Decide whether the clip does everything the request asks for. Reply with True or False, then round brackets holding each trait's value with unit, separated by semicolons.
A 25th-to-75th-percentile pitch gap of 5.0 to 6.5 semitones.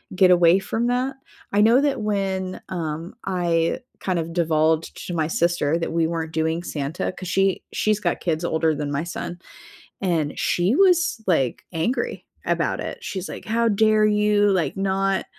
False (4.2 semitones)